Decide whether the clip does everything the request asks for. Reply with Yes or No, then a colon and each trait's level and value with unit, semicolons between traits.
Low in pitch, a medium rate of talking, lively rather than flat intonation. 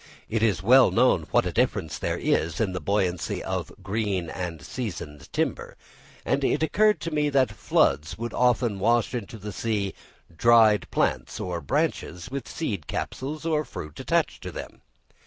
Yes: low, 110 Hz; average, 165 wpm; wide, 6.3 semitones